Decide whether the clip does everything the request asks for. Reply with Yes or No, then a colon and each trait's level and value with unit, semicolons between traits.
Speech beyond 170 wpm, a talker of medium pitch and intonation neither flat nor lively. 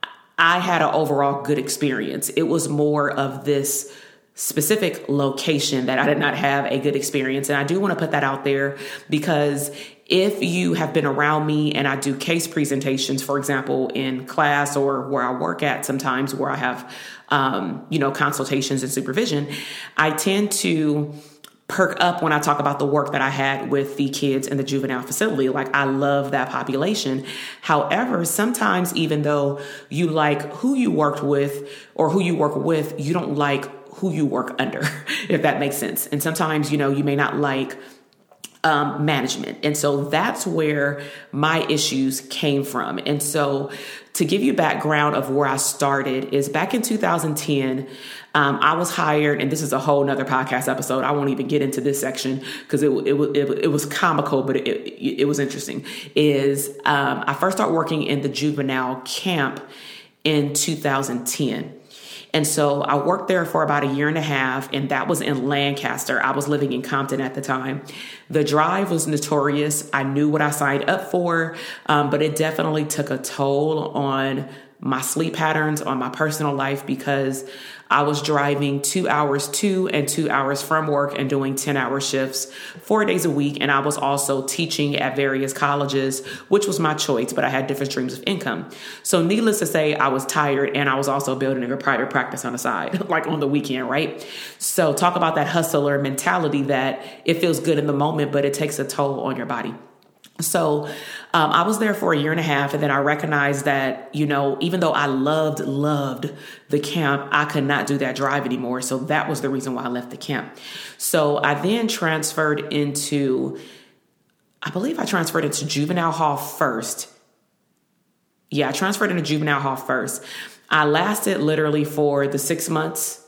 No: average, 190 wpm; medium, 145 Hz; narrow, 2.0 semitones